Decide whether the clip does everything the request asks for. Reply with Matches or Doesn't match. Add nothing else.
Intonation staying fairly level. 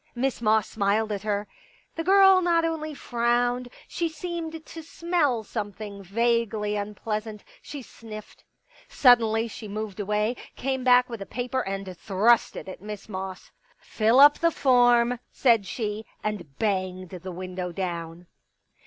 Doesn't match